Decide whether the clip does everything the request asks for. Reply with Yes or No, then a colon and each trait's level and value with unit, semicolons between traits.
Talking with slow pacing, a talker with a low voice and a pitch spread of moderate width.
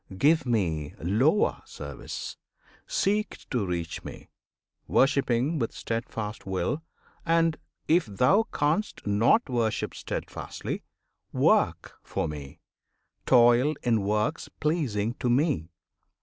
No: slow, 105 wpm; low, 120 Hz; wide, 6.9 semitones